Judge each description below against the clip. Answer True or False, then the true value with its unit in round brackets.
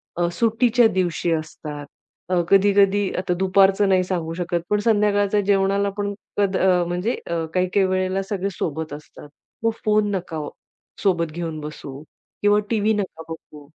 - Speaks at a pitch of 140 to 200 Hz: True (190 Hz)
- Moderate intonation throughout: True (3.2 semitones)